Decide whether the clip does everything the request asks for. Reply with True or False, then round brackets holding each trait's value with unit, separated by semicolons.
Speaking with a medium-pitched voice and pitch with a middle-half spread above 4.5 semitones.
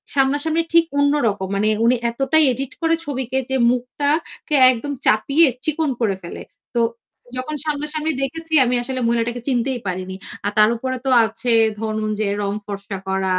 False (255 Hz; 5.2 semitones)